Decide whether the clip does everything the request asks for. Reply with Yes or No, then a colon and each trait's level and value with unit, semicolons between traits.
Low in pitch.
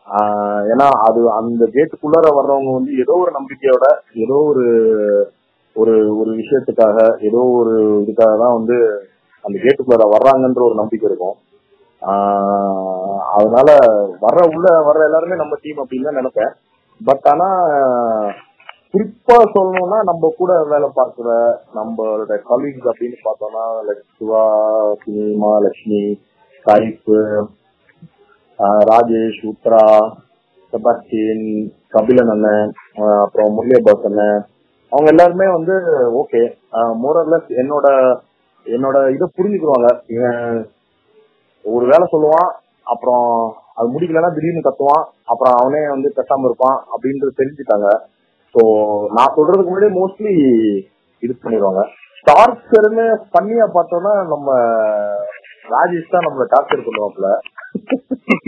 Yes: low, 125 Hz